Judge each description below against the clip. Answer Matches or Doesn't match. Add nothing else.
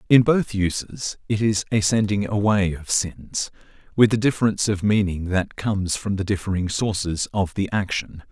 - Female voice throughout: Doesn't match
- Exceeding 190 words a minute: Doesn't match